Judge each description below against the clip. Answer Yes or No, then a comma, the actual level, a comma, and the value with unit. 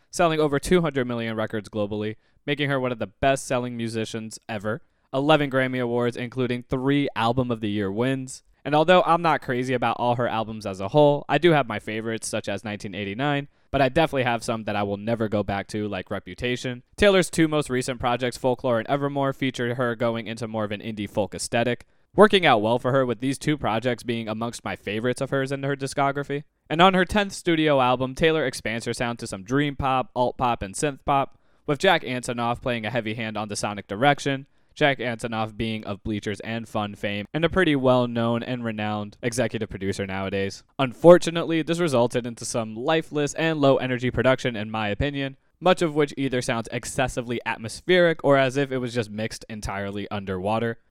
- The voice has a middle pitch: No, low, 125 Hz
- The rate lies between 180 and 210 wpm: Yes, fast, 205 wpm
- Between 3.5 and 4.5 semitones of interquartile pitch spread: Yes, average, 4.0 semitones